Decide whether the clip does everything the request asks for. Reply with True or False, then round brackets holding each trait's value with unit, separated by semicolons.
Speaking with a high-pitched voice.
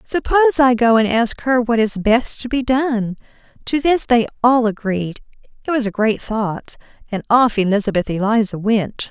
True (230 Hz)